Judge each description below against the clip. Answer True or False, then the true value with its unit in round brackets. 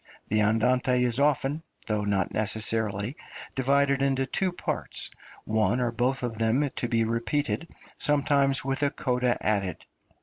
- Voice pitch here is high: False (125 Hz)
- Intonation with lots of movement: False (3.8 semitones)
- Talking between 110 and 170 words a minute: True (140 wpm)